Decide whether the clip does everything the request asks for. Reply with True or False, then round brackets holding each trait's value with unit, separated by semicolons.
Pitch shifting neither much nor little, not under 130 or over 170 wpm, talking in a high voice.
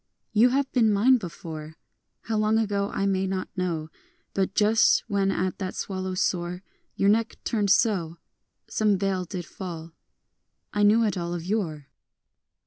True (3.0 semitones; 165 wpm; 195 Hz)